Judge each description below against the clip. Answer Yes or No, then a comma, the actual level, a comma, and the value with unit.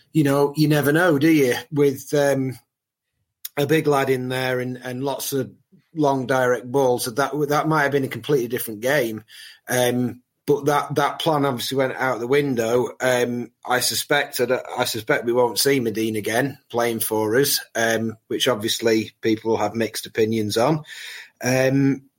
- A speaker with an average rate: Yes, average, 170 wpm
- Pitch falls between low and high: No, low, 130 Hz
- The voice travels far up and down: No, average, 3.2 semitones